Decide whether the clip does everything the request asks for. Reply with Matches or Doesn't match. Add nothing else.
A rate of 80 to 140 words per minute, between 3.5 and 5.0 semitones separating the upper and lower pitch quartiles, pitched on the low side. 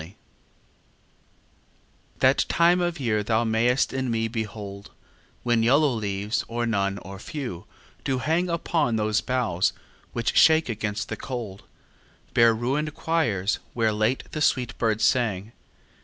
Matches